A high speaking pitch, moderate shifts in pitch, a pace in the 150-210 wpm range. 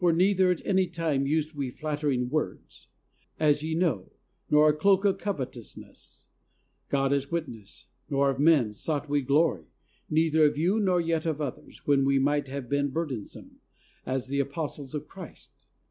No: medium, 150 Hz; average, 3.1 semitones; average, 165 wpm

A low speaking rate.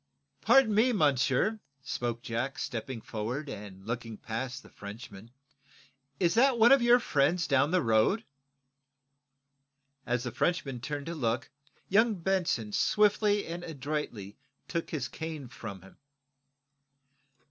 Yes: slow, 125 wpm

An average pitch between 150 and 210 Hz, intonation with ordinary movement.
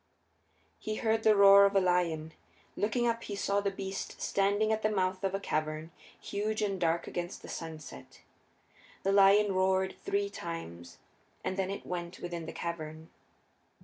Yes: high, 190 Hz; average, 3.2 semitones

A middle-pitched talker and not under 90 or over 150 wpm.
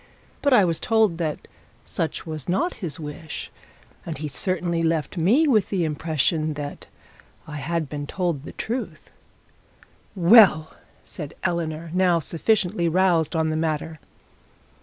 Yes: medium, 165 Hz; average, 140 wpm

